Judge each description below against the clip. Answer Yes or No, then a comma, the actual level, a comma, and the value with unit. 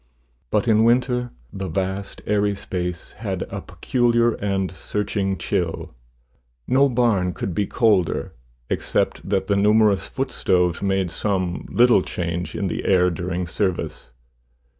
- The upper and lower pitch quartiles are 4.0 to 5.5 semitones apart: No, average, 3.2 semitones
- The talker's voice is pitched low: Yes, low, 100 Hz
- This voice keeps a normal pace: No, slow, 130 wpm